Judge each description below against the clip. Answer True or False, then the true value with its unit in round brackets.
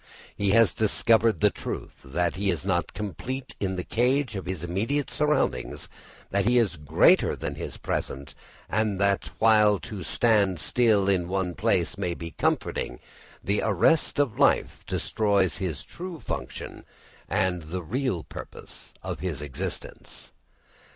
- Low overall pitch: True (100 Hz)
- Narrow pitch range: False (4.3 semitones)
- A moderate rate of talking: True (145 wpm)